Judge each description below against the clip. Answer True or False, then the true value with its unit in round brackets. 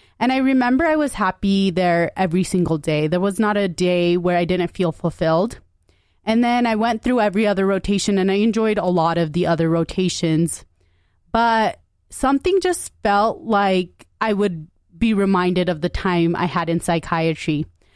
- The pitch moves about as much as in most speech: True (4.1 semitones)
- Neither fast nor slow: True (175 wpm)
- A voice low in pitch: False (180 Hz)